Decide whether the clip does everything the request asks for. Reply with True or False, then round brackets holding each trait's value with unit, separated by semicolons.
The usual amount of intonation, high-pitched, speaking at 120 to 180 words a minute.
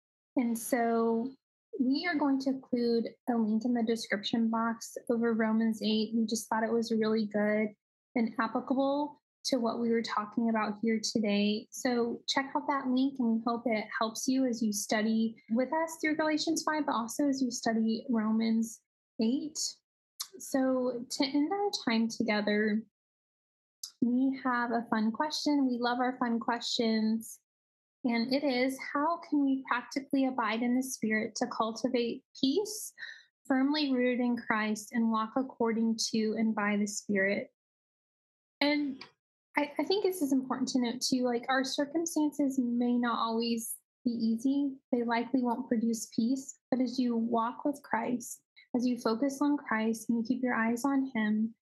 True (3.0 semitones; 240 Hz; 165 wpm)